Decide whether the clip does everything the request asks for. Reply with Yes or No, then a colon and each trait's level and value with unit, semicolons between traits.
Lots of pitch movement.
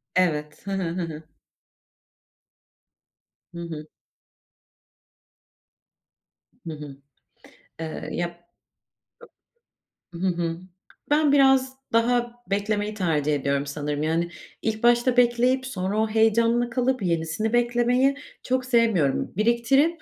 Yes: wide, 6.5 semitones